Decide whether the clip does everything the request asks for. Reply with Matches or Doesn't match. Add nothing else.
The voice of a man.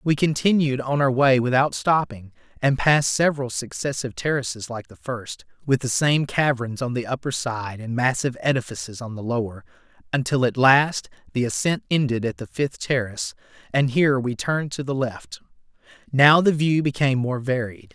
Matches